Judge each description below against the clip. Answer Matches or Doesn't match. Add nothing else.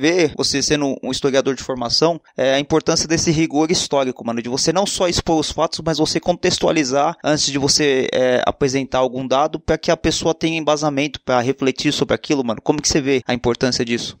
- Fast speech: Matches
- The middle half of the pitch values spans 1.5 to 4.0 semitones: Matches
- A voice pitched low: Doesn't match